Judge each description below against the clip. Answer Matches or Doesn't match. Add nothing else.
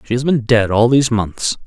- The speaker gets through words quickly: Matches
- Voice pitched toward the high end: Doesn't match